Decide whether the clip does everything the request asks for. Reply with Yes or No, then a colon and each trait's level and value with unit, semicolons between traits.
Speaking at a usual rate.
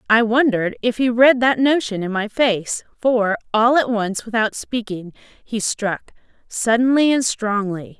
Yes: average, 160 wpm